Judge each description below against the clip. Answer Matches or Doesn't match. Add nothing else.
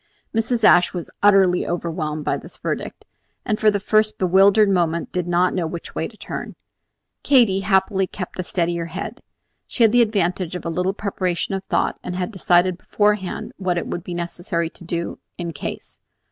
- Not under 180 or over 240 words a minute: Matches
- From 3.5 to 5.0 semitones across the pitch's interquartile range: Doesn't match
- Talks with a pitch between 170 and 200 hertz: Matches